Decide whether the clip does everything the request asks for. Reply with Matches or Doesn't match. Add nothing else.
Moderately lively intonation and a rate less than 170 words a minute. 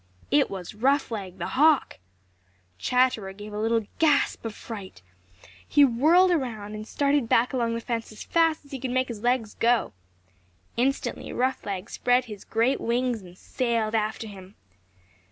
Matches